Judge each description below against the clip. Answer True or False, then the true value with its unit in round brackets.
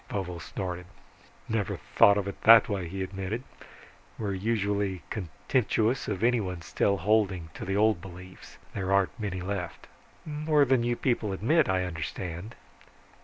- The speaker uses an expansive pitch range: False (3.3 semitones)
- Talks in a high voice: False (100 Hz)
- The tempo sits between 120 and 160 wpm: True (145 wpm)